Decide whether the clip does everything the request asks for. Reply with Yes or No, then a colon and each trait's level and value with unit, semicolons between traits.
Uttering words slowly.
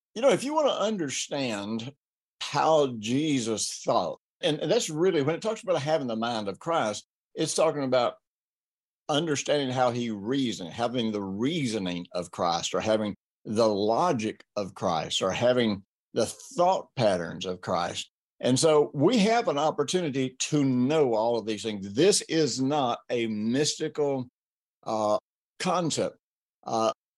No: average, 150 wpm